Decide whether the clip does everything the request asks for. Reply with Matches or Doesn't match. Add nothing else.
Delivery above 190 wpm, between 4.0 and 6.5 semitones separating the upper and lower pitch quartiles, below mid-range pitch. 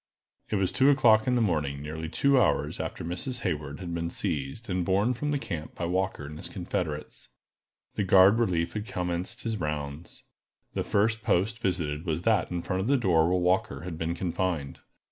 Matches